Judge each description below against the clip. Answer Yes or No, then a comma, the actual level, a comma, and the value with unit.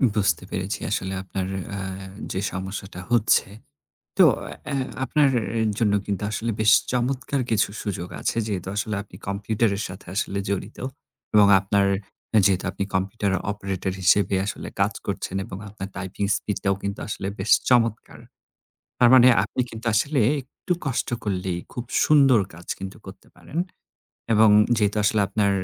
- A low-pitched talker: Yes, low, 100 Hz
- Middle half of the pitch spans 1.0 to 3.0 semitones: Yes, average, 2.7 semitones